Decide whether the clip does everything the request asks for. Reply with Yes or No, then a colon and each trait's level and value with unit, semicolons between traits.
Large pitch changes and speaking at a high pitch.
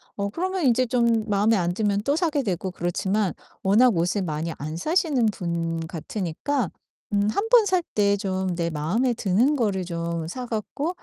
Yes: wide, 6.4 semitones; high, 205 Hz